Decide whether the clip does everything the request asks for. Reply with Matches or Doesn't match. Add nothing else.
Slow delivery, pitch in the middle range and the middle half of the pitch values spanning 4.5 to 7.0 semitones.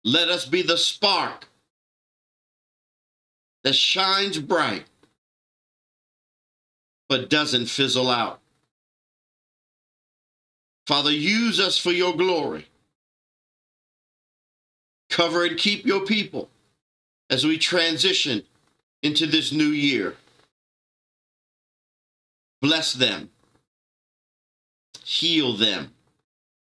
Matches